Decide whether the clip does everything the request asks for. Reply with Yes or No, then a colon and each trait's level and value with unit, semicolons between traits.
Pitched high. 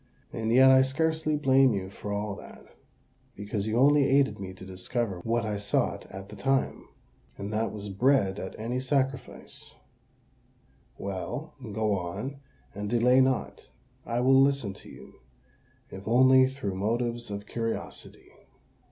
No: low, 115 Hz